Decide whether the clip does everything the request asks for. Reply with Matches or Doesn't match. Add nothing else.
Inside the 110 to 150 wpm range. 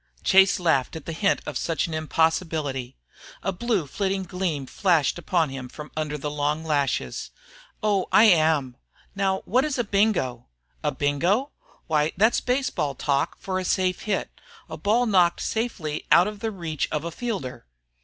Doesn't match